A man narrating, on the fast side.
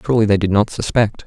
Yes: male; fast, 235 wpm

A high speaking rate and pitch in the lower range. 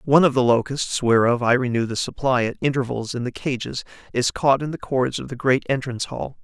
Yes: fast, 225 wpm; low, 130 Hz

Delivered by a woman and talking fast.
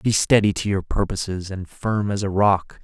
No: male; fast, 210 wpm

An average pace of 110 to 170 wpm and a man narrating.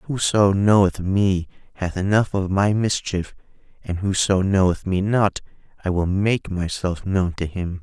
Yes: average, 155 wpm; male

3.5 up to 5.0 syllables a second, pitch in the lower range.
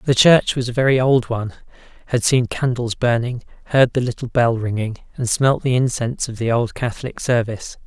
No: 5.6 syllables/s; low, 120 Hz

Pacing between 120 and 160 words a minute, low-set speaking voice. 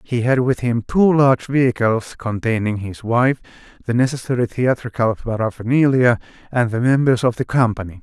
Yes: average, 150 wpm; low, 120 Hz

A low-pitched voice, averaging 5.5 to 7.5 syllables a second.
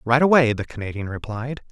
Yes: low, 125 Hz; 5.7 syllables/s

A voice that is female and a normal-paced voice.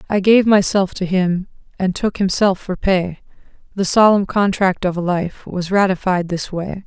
Yes: female; average, 175 wpm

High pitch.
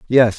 No: low, 120 Hz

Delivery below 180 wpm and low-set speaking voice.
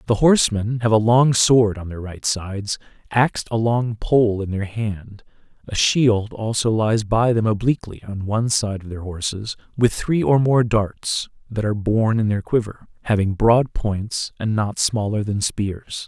No: average, 185 wpm; low, 110 Hz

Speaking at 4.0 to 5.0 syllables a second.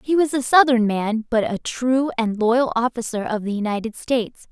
Yes: 4.9 syllables/s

